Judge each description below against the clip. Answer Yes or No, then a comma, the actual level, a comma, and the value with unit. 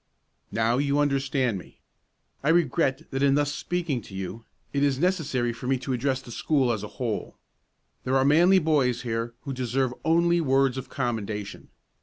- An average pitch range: Yes, average, 3.3 semitones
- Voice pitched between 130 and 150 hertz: Yes, low, 135 Hz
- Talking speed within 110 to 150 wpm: No, average, 175 wpm